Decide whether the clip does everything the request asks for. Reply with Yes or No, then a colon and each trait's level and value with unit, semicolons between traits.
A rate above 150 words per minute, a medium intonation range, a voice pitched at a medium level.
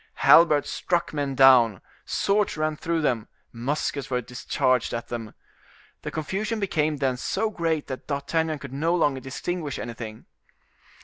No: average, 140 wpm; average, 4.3 semitones; medium, 145 Hz